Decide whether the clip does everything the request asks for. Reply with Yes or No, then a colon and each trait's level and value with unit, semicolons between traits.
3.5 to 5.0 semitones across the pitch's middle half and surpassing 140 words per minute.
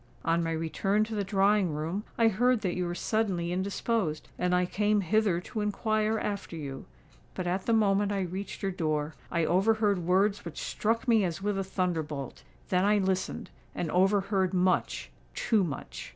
No: average, 3.1 semitones; average, 170 wpm